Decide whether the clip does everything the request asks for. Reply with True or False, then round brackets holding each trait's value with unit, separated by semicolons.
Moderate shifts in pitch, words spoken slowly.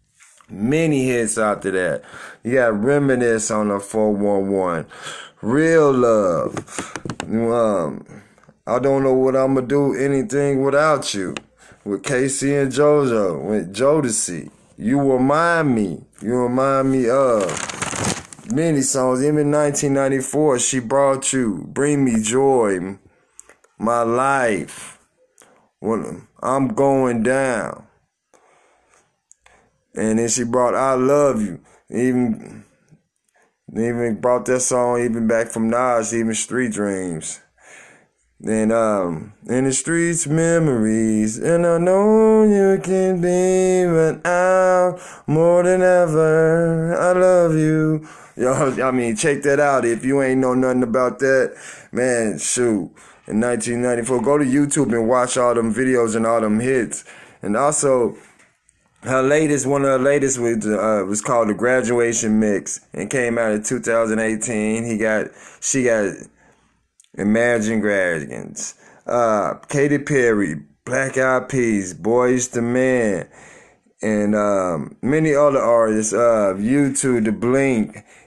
True (3.9 semitones; 125 wpm)